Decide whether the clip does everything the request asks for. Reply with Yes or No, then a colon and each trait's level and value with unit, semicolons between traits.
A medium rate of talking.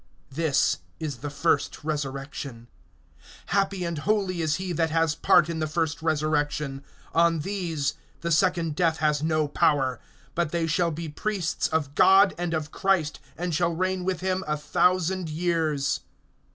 Yes: average, 155 wpm